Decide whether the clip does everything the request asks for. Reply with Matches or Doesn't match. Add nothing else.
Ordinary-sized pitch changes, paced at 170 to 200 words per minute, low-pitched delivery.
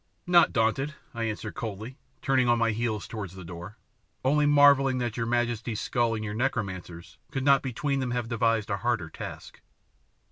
Matches